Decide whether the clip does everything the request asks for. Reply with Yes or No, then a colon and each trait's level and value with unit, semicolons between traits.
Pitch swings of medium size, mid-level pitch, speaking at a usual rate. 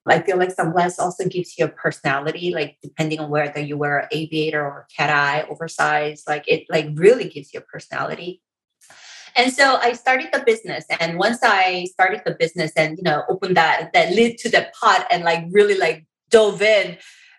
No: wide, 5.8 semitones; medium, 170 Hz; average, 195 wpm